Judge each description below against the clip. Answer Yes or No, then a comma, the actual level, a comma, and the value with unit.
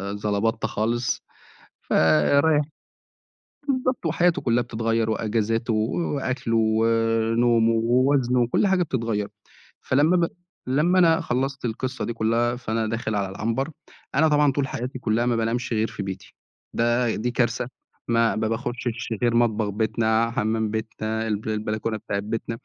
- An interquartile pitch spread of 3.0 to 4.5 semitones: No, narrow, 2.4 semitones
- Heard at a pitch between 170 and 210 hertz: No, low, 115 Hz